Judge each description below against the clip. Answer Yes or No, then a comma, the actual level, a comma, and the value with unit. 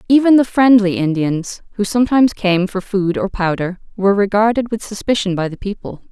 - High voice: Yes, high, 205 Hz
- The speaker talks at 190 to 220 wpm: No, average, 175 wpm